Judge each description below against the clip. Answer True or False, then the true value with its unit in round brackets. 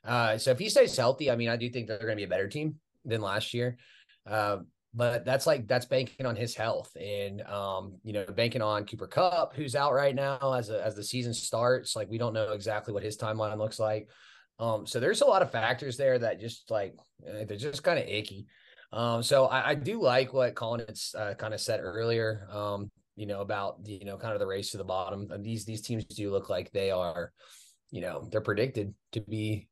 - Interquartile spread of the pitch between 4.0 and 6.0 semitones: False (2.8 semitones)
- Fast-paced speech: True (235 wpm)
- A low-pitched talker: True (110 Hz)